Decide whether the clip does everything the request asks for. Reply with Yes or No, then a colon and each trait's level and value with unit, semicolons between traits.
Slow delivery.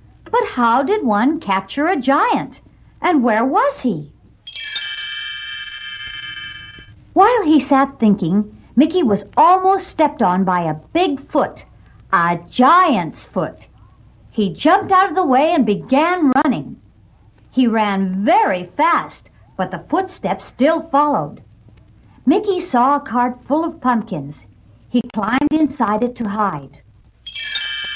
Yes: slow, 125 wpm